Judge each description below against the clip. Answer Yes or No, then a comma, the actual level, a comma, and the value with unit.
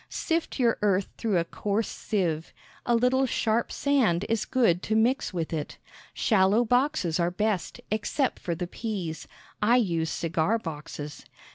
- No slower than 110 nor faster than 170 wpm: Yes, average, 150 wpm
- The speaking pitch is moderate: No, high, 210 Hz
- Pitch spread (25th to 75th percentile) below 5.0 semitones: No, wide, 5.6 semitones